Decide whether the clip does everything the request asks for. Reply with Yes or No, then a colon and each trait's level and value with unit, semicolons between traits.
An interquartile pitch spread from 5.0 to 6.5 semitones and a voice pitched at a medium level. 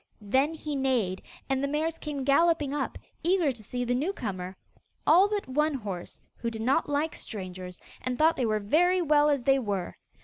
No: wide, 5.5 semitones; very high, 275 Hz